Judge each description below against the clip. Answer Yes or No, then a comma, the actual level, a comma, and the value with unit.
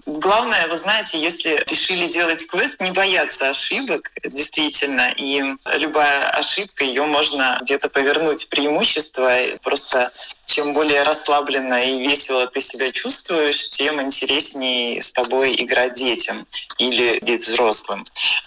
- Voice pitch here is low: No, medium, 145 Hz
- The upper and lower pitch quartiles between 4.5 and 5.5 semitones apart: No, average, 2.9 semitones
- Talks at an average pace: Yes, average, 125 wpm